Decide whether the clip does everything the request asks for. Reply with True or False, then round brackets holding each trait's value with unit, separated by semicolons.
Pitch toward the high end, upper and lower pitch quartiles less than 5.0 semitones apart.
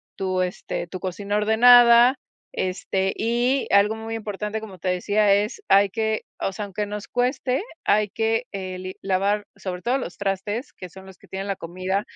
True (205 Hz; 2.8 semitones)